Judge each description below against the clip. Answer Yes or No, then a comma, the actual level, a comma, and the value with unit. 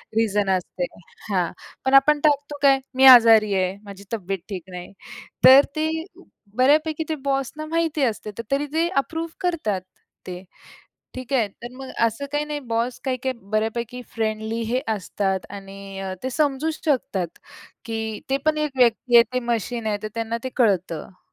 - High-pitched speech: Yes, high, 235 Hz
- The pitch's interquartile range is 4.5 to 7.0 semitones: Yes, wide, 5.5 semitones